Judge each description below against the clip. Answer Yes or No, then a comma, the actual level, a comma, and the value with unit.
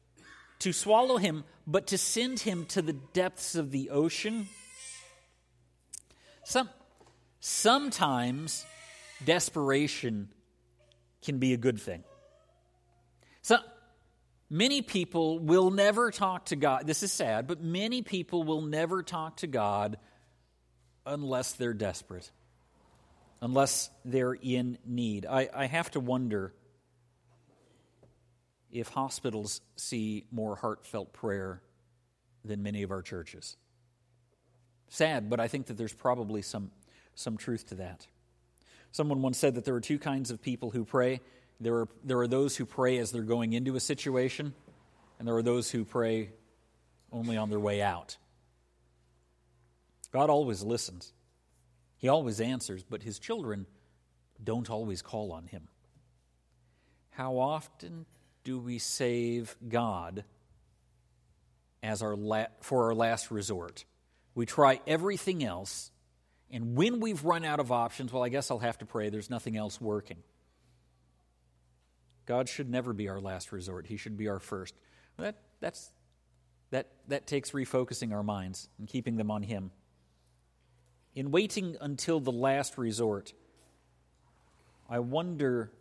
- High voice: No, low, 120 Hz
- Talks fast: No, slow, 135 wpm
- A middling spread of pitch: No, wide, 6.9 semitones